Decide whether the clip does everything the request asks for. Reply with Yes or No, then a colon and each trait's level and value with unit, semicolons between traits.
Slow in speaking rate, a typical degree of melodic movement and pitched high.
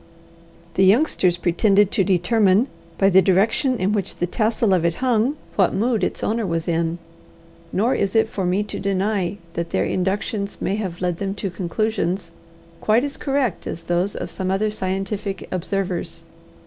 No: average, 170 wpm; average, 3.0 semitones; high, 195 Hz